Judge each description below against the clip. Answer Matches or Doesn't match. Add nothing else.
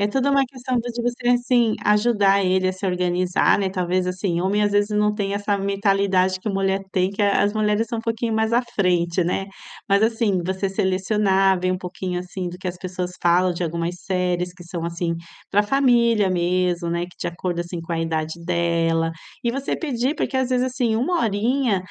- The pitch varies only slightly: Doesn't match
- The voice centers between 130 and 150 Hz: Doesn't match